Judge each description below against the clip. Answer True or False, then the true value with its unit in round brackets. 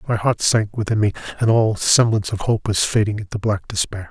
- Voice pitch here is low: True (105 Hz)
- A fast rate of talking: True (220 wpm)